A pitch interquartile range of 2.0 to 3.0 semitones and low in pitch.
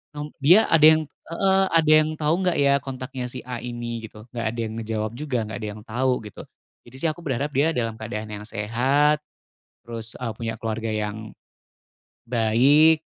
No: average, 4.9 semitones; low, 125 Hz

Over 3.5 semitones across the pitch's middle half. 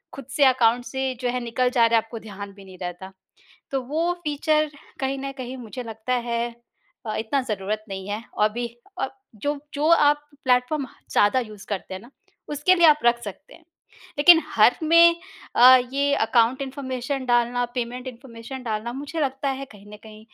Yes: average, 4.0 semitones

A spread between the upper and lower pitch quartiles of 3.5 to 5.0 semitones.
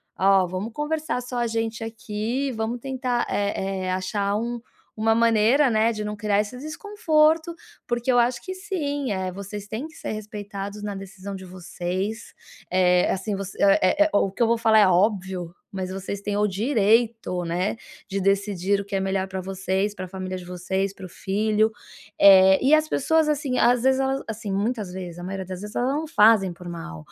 Yes: average, 4.0 semitones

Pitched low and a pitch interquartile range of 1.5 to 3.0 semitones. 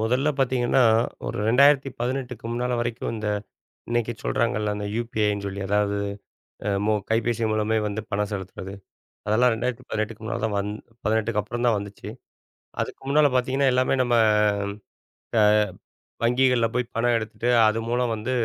Yes: low, 115 Hz; average, 2.7 semitones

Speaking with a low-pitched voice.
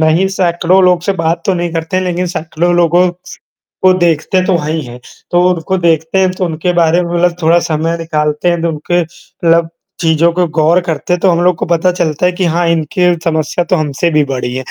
No: medium, 170 Hz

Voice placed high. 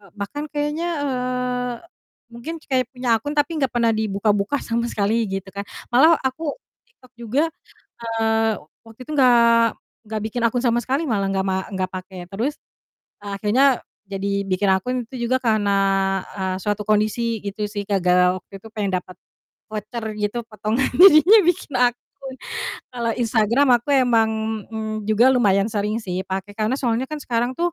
Yes: high, 225 Hz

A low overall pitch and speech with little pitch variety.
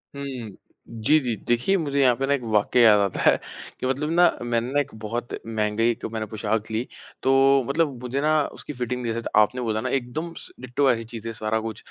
No: low, 120 Hz; average, 3.7 semitones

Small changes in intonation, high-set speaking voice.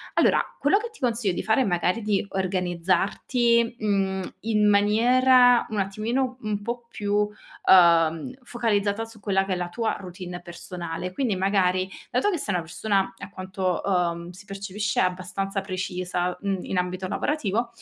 No: average, 3.7 semitones; high, 195 Hz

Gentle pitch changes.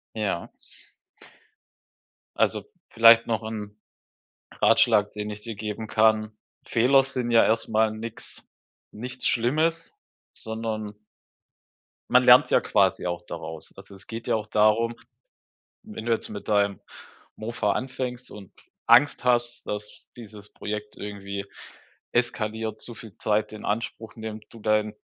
Yes: narrow, 1.9 semitones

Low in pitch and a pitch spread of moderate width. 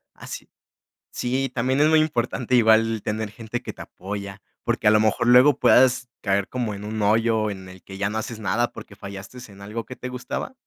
Yes: low, 110 Hz; average, 3.5 semitones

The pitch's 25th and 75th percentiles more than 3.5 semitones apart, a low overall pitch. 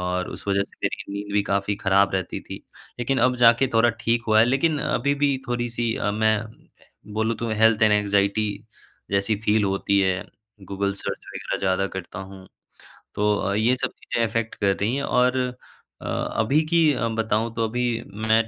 No: average, 2.9 semitones; low, 110 Hz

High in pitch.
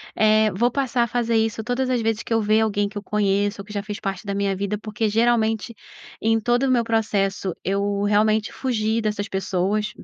Yes: high, 215 Hz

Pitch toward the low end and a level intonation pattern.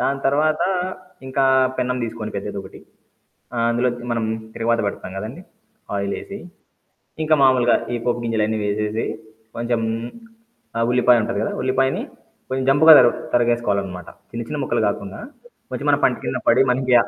No: low, 120 Hz; average, 3.2 semitones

